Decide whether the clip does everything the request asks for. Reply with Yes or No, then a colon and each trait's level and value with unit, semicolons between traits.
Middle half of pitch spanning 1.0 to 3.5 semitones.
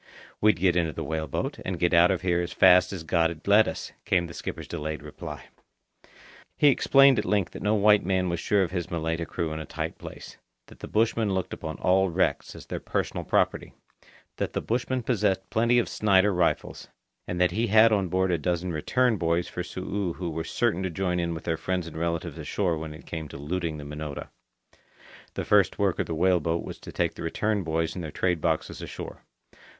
Yes: average, 3.2 semitones